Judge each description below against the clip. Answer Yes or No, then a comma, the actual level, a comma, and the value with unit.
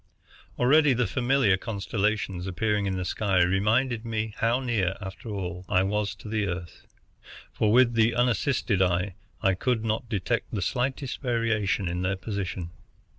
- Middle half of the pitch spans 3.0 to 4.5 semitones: Yes, average, 3.7 semitones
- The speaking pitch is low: Yes, low, 105 Hz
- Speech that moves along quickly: No, average, 155 wpm